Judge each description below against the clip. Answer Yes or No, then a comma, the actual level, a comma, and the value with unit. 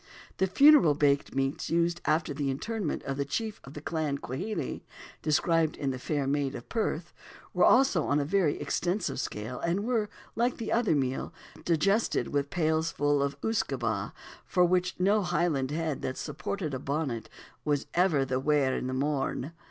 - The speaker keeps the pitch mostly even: No, average, 4.5 semitones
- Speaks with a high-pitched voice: No, medium, 155 Hz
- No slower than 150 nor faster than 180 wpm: Yes, average, 170 wpm